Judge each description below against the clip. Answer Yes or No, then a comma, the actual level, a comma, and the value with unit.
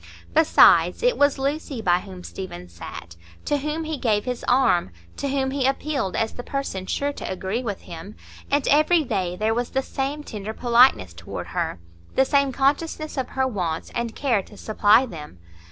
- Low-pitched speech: No, high, 245 Hz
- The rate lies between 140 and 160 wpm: No, average, 185 wpm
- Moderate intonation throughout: No, wide, 6.5 semitones